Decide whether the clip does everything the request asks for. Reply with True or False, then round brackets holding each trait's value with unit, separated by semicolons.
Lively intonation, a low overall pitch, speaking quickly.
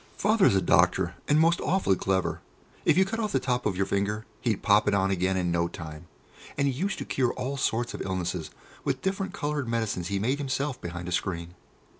True (7.3 semitones; 105 Hz; 220 wpm)